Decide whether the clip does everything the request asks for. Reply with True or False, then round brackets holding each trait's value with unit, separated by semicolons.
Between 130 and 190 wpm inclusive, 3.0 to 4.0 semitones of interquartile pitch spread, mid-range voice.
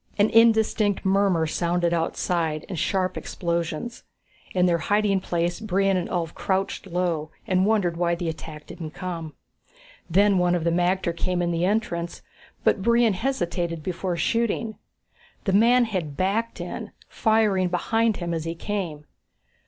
True (150 wpm; 3.3 semitones; 180 Hz)